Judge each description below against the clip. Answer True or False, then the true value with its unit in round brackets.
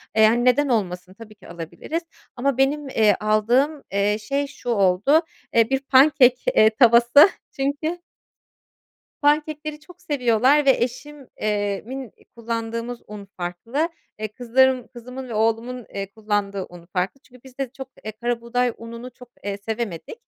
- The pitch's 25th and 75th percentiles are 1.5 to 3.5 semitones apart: False (4.1 semitones)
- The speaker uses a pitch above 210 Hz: True (240 Hz)